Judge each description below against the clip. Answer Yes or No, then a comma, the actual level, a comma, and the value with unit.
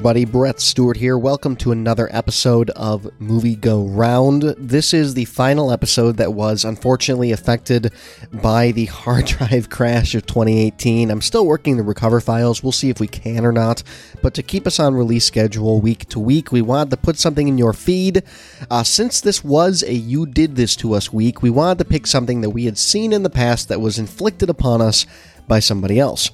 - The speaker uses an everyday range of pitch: Yes, average, 3.6 semitones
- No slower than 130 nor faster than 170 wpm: No, fast, 205 wpm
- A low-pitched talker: Yes, low, 120 Hz